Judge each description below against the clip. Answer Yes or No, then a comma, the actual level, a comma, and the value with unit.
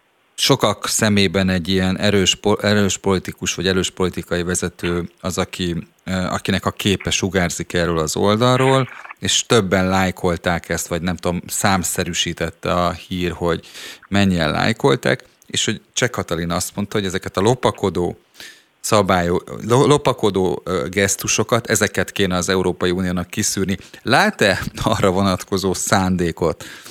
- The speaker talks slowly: No, average, 125 wpm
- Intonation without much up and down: Yes, narrow, 2.3 semitones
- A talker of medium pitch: No, very low, 95 Hz